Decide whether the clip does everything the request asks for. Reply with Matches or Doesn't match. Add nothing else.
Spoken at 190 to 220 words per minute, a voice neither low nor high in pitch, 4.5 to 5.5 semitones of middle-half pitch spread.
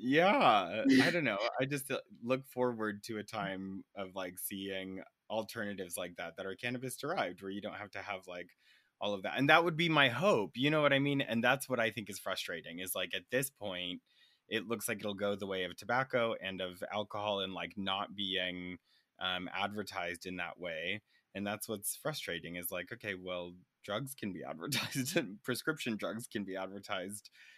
Doesn't match